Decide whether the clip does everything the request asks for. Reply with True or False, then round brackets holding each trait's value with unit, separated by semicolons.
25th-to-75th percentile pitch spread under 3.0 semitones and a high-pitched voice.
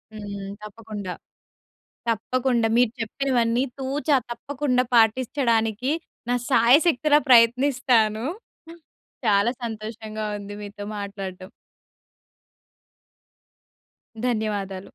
False (3.4 semitones; 225 Hz)